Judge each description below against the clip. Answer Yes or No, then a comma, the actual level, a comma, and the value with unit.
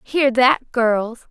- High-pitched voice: Yes, high, 245 Hz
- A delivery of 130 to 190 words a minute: Yes, average, 140 wpm